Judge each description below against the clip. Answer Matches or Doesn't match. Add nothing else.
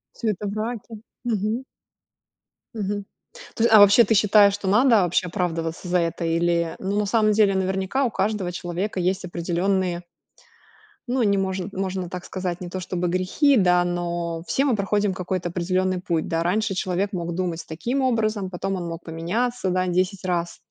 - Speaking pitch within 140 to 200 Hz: Matches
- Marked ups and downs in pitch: Doesn't match